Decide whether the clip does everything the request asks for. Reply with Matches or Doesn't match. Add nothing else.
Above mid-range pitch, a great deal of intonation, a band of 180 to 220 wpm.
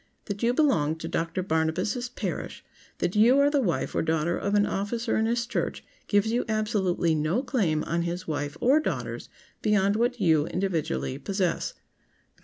Doesn't match